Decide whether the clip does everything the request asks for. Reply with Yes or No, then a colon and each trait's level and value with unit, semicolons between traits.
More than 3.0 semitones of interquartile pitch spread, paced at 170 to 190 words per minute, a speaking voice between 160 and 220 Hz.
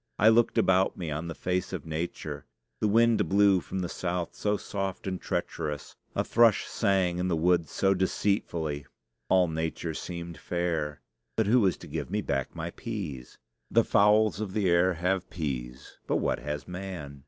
No: average, 3.6 semitones; average, 175 wpm; very low, 90 Hz